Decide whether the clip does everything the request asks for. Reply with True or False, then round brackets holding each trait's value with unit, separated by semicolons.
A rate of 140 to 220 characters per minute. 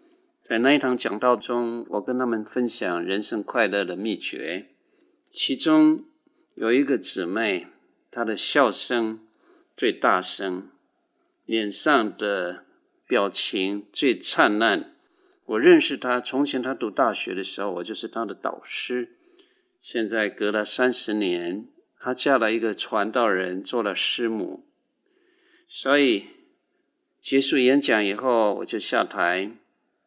True (185 characters per minute)